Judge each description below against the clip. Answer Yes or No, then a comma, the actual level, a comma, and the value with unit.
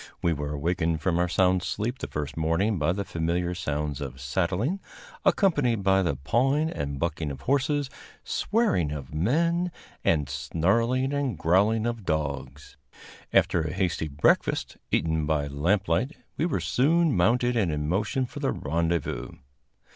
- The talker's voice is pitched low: Yes, very low, 90 Hz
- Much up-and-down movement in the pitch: Yes, wide, 7.7 semitones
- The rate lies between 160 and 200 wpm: No, average, 150 wpm